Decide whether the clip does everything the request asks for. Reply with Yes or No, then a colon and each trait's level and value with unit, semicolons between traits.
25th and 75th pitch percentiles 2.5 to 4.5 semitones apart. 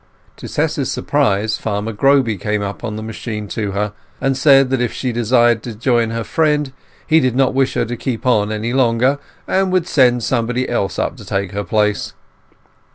Yes: average, 3.7 semitones